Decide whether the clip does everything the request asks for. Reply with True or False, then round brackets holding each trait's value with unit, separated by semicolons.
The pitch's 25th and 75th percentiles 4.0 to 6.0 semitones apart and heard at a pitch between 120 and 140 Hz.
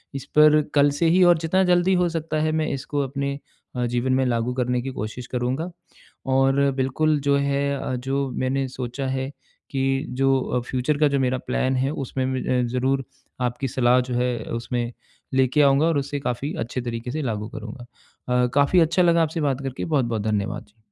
False (2.6 semitones; 135 Hz)